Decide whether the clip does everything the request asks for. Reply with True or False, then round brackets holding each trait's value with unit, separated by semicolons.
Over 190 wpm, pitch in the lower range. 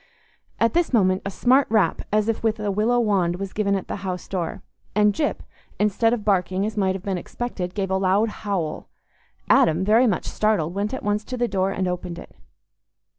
False (205 wpm; 200 Hz)